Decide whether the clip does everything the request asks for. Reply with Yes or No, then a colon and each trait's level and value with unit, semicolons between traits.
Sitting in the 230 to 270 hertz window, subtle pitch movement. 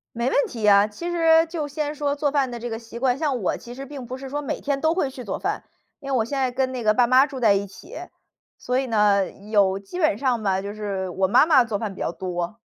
No: high, 245 Hz; wide, 5.4 semitones